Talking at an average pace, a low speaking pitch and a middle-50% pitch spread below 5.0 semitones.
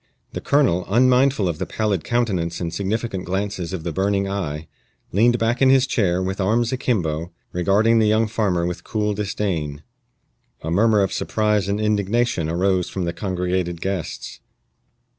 Yes: average, 160 wpm; low, 100 Hz; average, 3.9 semitones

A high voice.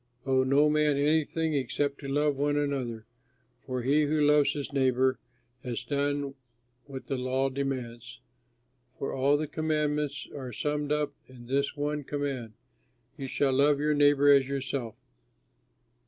No: medium, 140 Hz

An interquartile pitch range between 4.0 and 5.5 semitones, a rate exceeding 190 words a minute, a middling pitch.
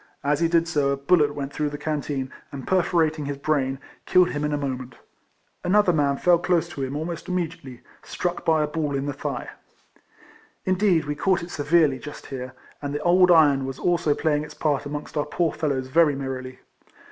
No: average, 3.3 semitones; average, 200 wpm; medium, 150 Hz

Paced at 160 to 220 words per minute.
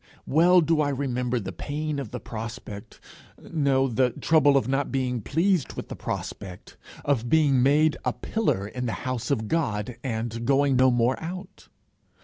Yes: average, 165 wpm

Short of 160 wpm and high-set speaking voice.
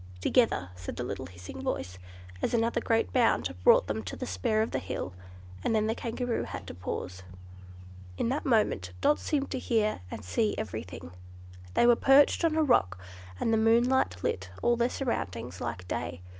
No: average, 185 wpm; high, 215 Hz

